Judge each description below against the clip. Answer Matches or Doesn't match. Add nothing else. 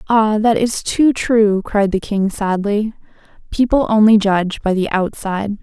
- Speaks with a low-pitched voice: Doesn't match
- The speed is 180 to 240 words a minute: Doesn't match